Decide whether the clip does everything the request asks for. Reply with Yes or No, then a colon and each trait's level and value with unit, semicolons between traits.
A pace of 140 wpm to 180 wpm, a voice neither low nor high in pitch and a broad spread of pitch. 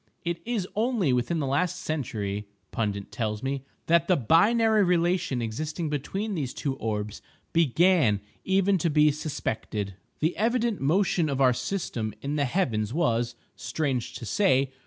Yes: average, 150 wpm; medium, 150 Hz; wide, 7.1 semitones